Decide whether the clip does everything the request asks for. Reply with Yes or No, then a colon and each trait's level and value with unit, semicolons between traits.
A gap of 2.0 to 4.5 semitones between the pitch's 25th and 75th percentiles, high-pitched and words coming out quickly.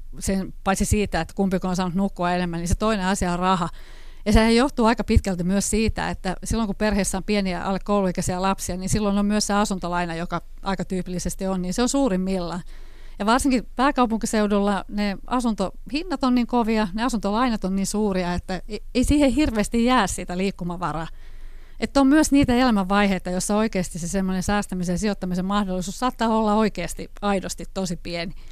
Yes: average, 3.4 semitones; high, 195 Hz; fast, 175 wpm